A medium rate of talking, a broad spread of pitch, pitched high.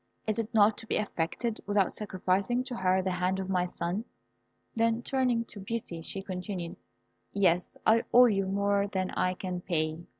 No: average, 175 wpm; average, 3.5 semitones; high, 195 Hz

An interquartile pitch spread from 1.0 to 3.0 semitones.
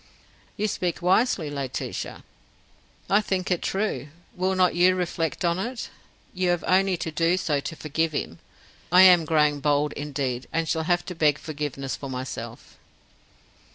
No: average, 3.9 semitones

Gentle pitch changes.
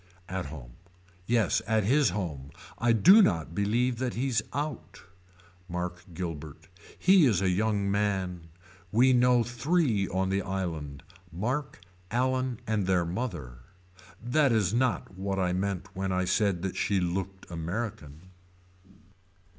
No: average, 5.2 semitones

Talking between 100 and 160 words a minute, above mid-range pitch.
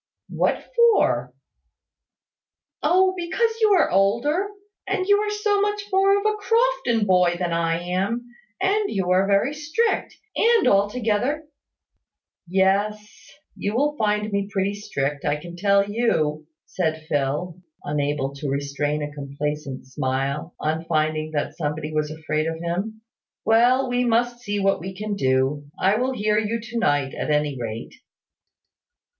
Yes: average, 150 wpm; high, 195 Hz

